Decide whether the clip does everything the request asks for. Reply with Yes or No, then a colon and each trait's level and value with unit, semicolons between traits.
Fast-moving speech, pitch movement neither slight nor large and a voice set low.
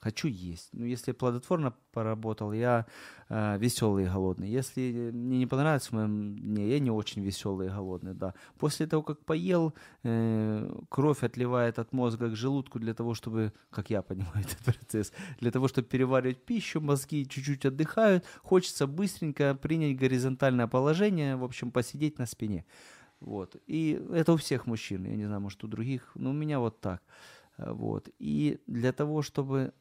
Yes: fast, 170 wpm; average, 4.7 semitones; low, 125 Hz